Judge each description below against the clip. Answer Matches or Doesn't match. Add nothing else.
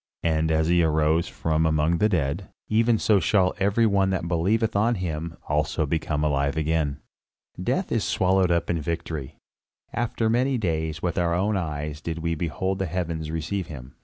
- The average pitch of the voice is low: Matches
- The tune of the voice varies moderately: Matches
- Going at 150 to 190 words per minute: Matches